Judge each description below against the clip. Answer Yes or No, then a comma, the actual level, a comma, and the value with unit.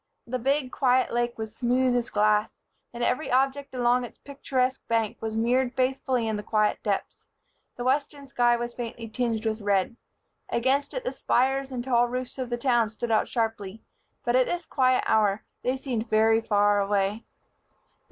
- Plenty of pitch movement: No, average, 2.7 semitones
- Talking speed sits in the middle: Yes, average, 175 wpm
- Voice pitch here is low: No, high, 240 Hz